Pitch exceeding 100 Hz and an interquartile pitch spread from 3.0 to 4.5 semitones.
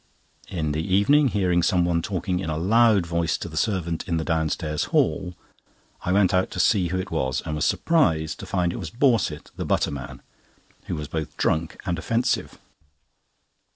No: very low, 85 Hz; average, 3.3 semitones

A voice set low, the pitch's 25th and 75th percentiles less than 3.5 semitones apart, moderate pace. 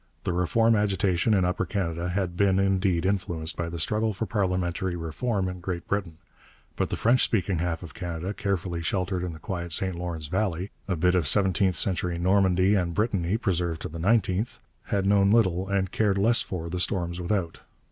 Yes: very low, 95 Hz; narrow, 2.5 semitones; average, 190 wpm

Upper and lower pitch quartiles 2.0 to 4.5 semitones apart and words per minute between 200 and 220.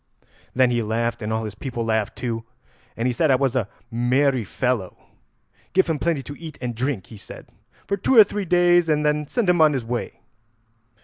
No: average, 5.3 semitones; fast, 205 wpm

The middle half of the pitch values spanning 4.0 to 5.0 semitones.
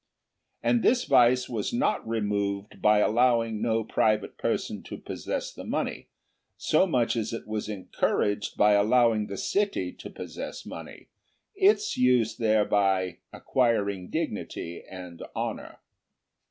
No: average, 3.3 semitones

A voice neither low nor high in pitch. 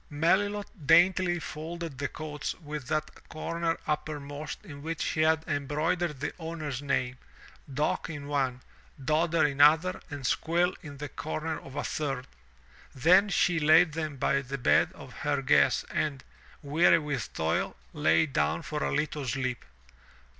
Yes: medium, 150 Hz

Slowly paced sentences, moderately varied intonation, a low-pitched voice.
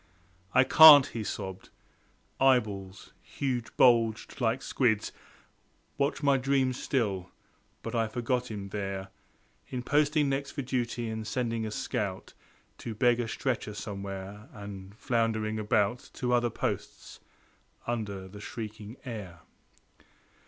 Yes: slow, 125 wpm; average, 3.6 semitones; low, 115 Hz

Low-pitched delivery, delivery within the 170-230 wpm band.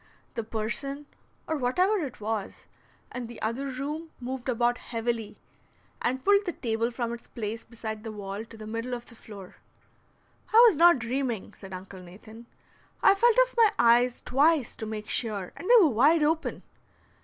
No: high, 240 Hz; average, 175 wpm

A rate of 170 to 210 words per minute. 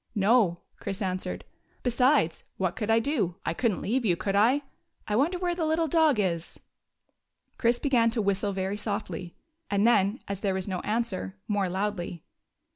Yes: average, 190 wpm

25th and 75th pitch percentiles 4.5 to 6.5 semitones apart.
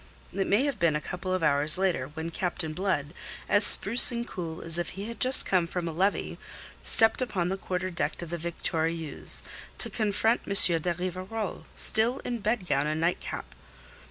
No: average, 3.8 semitones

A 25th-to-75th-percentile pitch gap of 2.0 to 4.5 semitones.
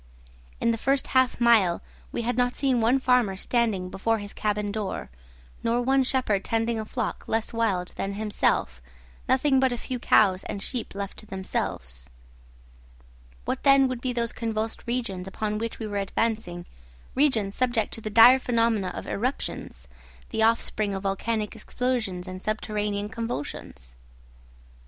Yes: average, 3.5 semitones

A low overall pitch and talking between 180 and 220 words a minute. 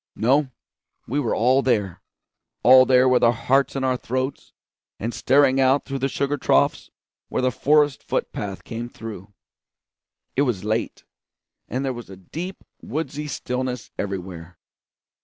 No: low, 130 Hz; average, 150 wpm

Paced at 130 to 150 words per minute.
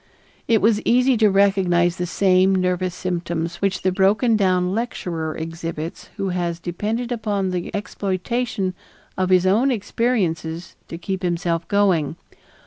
Yes: slow, 135 wpm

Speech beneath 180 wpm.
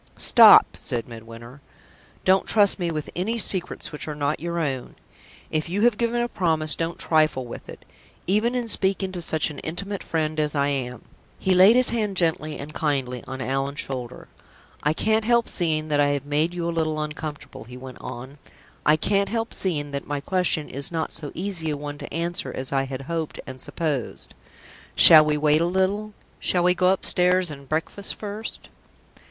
No: average, 190 wpm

